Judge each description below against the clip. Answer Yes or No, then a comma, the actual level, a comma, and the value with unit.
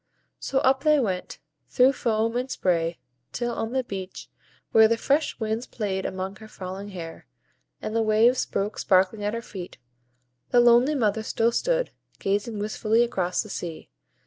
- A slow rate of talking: No, average, 165 wpm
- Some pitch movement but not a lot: Yes, average, 3.7 semitones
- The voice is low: No, high, 220 Hz